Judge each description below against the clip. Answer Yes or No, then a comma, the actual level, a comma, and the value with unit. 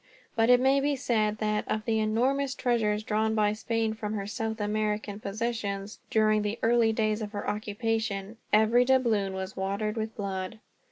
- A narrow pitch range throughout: Yes, narrow, 1.5 semitones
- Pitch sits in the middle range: No, high, 215 Hz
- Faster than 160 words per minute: Yes, average, 170 wpm